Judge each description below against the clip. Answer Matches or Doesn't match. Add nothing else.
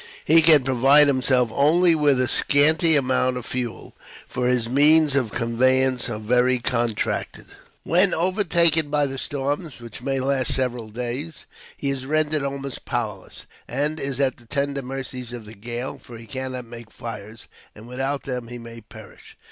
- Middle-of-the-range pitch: Doesn't match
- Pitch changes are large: Doesn't match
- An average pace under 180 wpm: Matches